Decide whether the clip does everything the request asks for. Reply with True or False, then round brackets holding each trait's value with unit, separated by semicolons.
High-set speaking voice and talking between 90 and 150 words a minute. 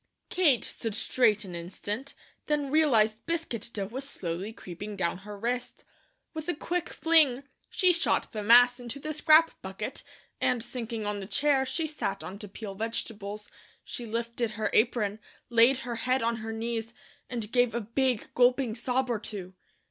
False (235 Hz; 170 wpm)